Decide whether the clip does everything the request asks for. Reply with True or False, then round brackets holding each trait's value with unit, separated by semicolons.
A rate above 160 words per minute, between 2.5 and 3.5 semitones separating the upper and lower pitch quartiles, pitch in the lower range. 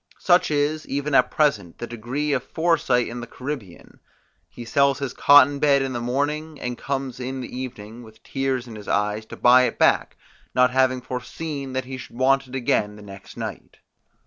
True (195 wpm; 2.9 semitones; 130 Hz)